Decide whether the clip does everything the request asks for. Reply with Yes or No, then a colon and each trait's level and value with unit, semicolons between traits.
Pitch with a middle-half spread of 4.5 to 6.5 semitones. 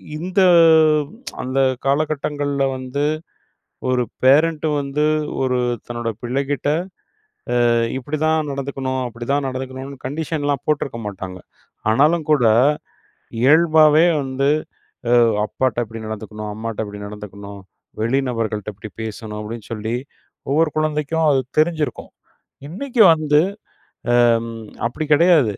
Yes: average, 4.8 semitones